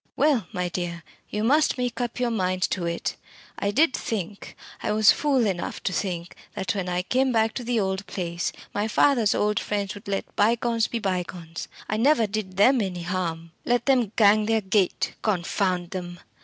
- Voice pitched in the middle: No, high, 205 Hz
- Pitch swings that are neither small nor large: Yes, average, 4.1 semitones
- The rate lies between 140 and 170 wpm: No, average, 185 wpm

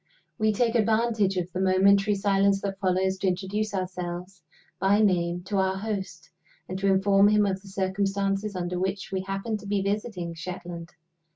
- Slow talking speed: No, average, 170 wpm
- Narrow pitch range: Yes, narrow, 1.6 semitones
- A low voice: No, high, 195 Hz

